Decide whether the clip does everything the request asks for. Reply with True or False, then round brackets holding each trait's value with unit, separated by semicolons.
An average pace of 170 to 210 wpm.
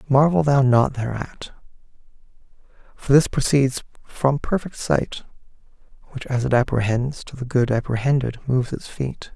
False (135 wpm)